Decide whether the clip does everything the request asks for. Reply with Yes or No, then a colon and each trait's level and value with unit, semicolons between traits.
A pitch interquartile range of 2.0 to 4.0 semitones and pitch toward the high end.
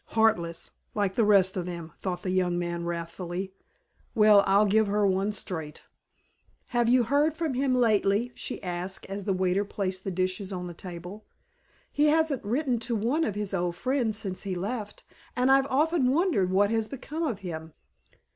No: average, 4.9 semitones; high, 200 Hz